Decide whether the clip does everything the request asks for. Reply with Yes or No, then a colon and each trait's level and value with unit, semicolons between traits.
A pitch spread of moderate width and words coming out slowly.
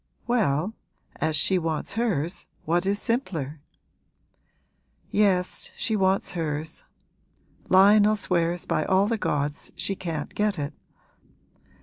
Yes: average, 4.5 semitones; slow, 110 wpm